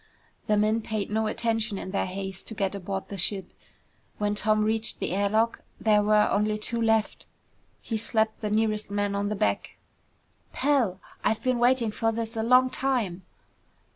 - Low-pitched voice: No, high, 215 Hz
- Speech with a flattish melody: Yes, narrow, 1.8 semitones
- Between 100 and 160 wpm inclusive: No, average, 175 wpm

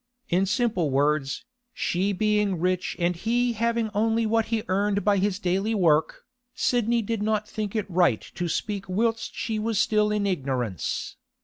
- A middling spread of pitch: Yes, average, 3.6 semitones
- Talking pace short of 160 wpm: No, average, 165 wpm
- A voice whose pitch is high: Yes, high, 205 Hz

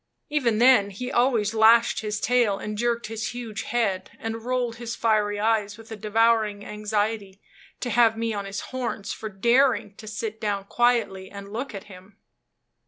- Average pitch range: No, narrow, 2.3 semitones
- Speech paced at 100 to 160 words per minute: No, average, 170 wpm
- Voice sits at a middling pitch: No, high, 220 Hz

